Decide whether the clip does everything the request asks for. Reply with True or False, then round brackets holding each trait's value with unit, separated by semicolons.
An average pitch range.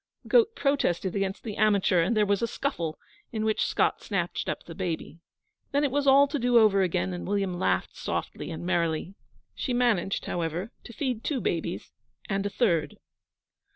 False (5.8 semitones)